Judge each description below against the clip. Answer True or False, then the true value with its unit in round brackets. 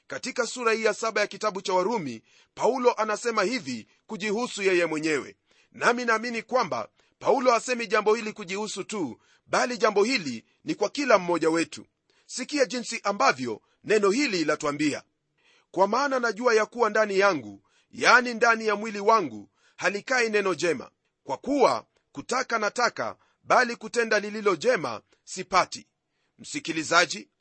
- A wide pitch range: False (3.5 semitones)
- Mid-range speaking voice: False (220 Hz)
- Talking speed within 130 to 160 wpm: True (140 wpm)